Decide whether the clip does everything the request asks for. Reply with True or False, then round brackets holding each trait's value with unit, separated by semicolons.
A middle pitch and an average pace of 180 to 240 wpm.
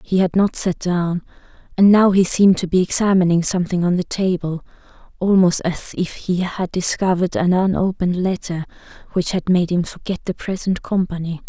False (180 Hz; 170 wpm)